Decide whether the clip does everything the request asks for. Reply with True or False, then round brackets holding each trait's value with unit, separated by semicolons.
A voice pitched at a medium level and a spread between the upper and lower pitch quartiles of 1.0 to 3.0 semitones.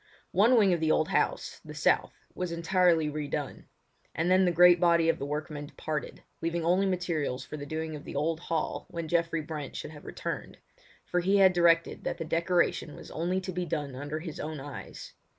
True (165 Hz; 2.6 semitones)